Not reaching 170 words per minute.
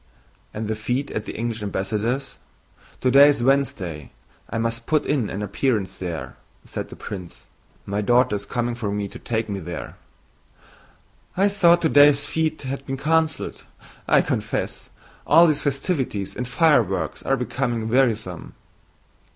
Yes: average, 145 wpm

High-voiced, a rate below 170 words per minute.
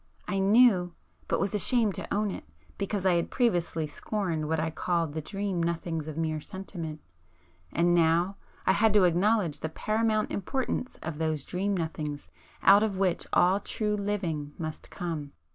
No: medium, 180 Hz; average, 160 wpm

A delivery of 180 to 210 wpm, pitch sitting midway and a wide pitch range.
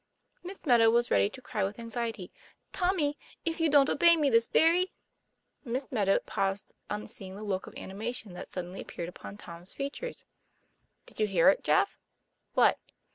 No: average, 185 wpm; high, 230 Hz; wide, 6.8 semitones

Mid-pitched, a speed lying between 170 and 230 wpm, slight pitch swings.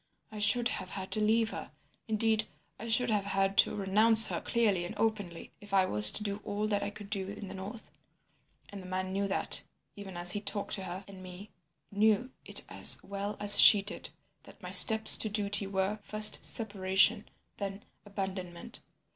No: high, 205 Hz; average, 190 wpm; narrow, 1.9 semitones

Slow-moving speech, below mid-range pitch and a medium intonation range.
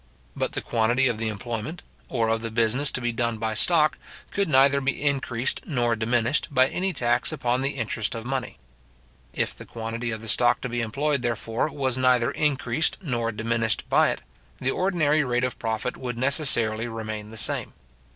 No: average, 185 wpm; low, 120 Hz; average, 3.2 semitones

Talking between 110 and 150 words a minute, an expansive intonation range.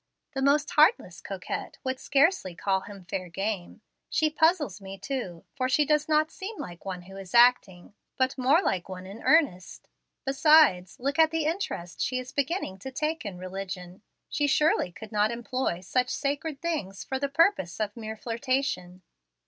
No: average, 175 wpm; wide, 7.7 semitones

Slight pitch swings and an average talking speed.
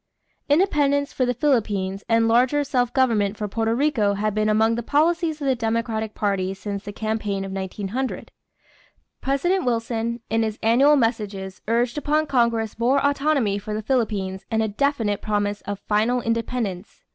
No: average, 4.1 semitones; average, 165 wpm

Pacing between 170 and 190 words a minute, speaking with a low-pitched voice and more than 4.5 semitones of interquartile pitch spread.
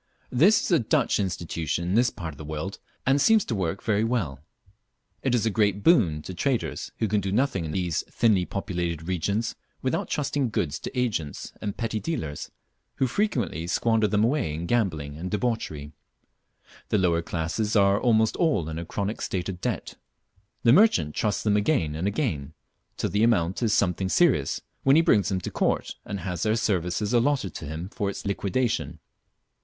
Yes: average, 180 wpm; low, 100 Hz; wide, 5.6 semitones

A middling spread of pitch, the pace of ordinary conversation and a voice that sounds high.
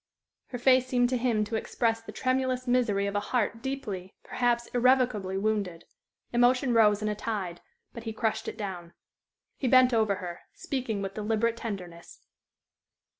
Yes: average, 3.5 semitones; average, 160 wpm; high, 225 Hz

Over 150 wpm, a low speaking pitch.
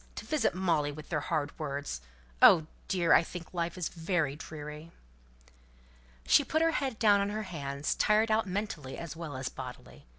No: average, 175 wpm; medium, 165 Hz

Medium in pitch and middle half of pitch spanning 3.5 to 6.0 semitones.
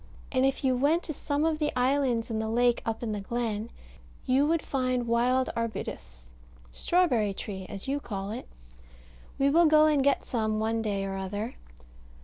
No: high, 245 Hz; average, 4.4 semitones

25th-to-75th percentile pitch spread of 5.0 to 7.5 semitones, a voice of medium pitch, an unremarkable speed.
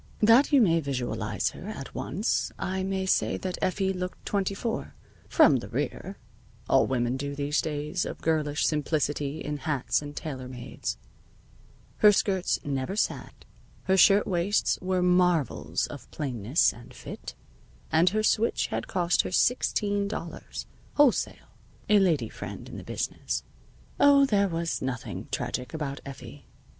Yes: wide, 5.5 semitones; medium, 170 Hz; average, 150 wpm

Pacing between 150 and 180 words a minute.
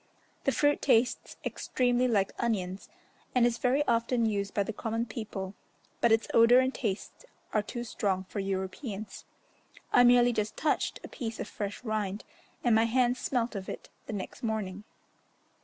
Yes: average, 165 wpm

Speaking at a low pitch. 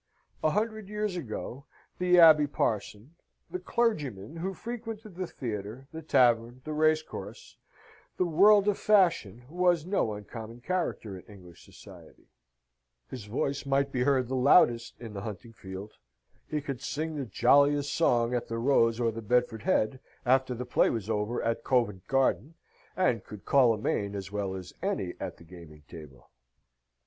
Yes: low, 125 Hz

